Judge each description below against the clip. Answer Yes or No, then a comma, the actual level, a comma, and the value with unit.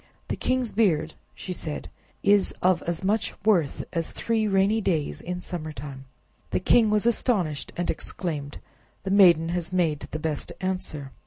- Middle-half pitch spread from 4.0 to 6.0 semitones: Yes, average, 4.5 semitones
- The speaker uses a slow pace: No, average, 160 wpm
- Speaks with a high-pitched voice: No, medium, 180 Hz